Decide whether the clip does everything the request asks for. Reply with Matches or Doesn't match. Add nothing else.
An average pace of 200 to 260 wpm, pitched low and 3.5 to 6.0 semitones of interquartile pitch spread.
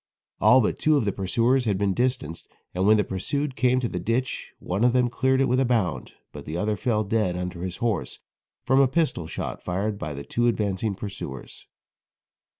Matches